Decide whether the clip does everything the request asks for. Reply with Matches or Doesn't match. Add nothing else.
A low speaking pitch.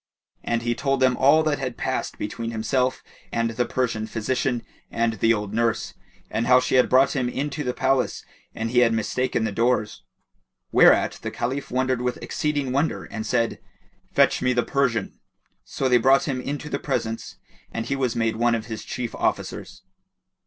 Matches